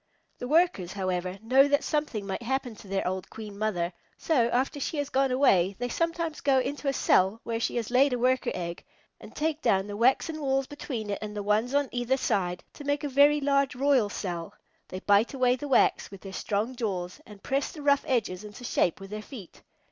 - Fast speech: Yes, fast, 215 wpm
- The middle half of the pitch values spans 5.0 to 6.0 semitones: Yes, wide, 5.6 semitones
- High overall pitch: Yes, high, 245 Hz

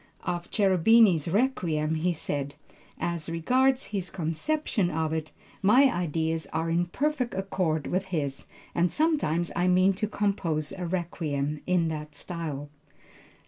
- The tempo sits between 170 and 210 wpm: No, slow, 135 wpm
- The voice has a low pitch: No, medium, 175 Hz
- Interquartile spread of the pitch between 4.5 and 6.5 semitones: No, average, 3.7 semitones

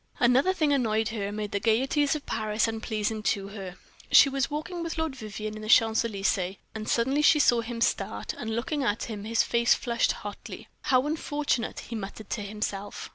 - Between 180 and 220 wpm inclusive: Yes, average, 195 wpm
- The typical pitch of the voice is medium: No, high, 225 Hz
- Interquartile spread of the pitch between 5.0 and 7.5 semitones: No, average, 4.2 semitones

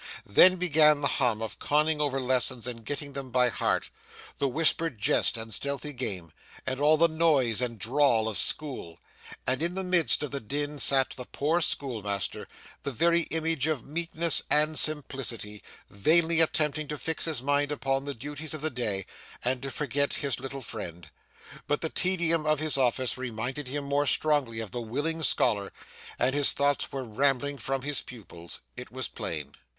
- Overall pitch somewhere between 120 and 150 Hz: Yes, medium, 140 Hz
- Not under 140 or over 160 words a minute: No, average, 175 wpm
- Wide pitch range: No, average, 3.8 semitones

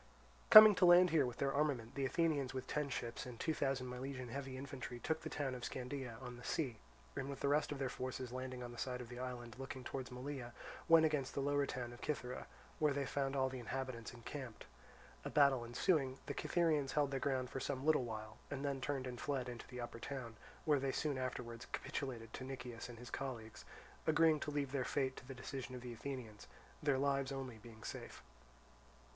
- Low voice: Yes, low, 130 Hz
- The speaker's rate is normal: No, fast, 215 wpm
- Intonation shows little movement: Yes, narrow, 2.3 semitones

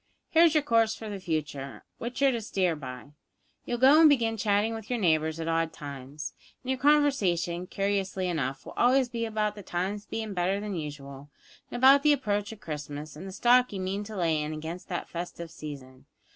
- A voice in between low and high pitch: No, high, 195 Hz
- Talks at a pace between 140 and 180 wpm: No, average, 200 wpm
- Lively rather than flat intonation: Yes, wide, 6.5 semitones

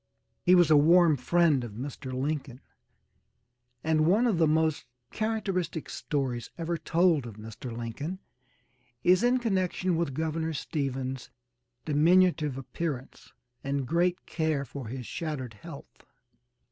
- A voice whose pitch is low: No, medium, 155 Hz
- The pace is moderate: No, slow, 125 wpm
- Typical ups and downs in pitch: Yes, average, 4.6 semitones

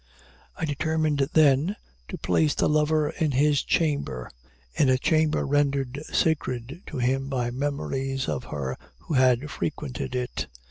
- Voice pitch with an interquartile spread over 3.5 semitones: No, average, 2.9 semitones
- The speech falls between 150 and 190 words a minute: No, average, 140 wpm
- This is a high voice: No, medium, 140 Hz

